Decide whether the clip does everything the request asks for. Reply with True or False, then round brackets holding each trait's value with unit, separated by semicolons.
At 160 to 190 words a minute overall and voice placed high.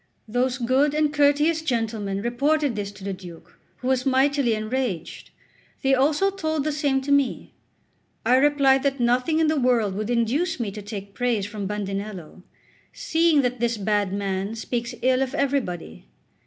True (165 wpm; 250 Hz)